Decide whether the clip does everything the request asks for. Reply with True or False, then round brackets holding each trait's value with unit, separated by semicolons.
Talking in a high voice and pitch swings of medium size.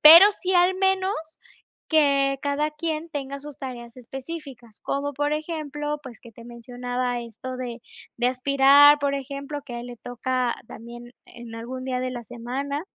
True (270 Hz; 3.3 semitones)